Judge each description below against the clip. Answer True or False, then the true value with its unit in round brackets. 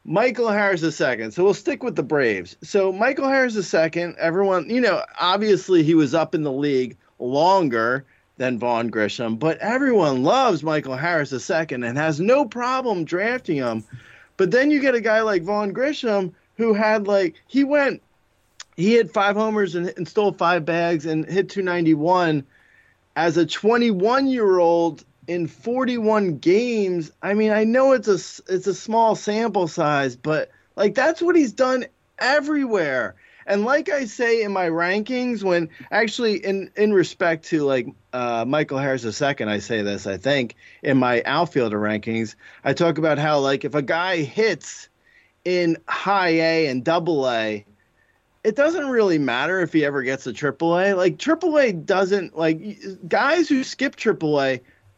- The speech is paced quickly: False (165 wpm)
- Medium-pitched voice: True (180 Hz)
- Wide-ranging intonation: True (6.6 semitones)